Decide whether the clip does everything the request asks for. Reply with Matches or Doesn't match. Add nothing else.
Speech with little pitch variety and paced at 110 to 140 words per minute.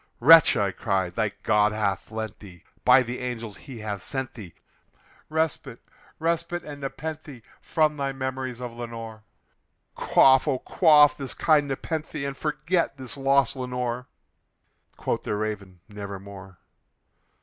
Doesn't match